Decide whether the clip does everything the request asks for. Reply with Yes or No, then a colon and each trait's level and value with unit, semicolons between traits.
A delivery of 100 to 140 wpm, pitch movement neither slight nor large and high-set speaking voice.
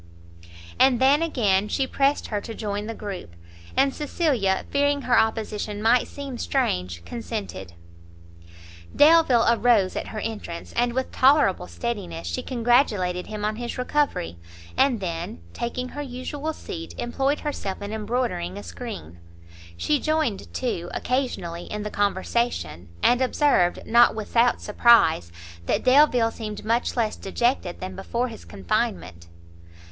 No: slow, 135 wpm; wide, 5.8 semitones; high, 225 Hz